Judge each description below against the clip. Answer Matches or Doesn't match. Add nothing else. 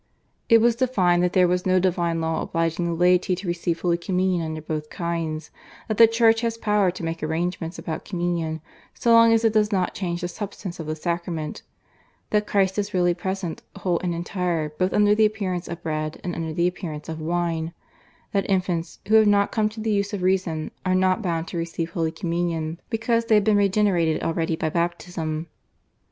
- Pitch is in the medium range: Matches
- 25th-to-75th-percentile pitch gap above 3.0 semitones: Matches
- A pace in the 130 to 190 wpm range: Doesn't match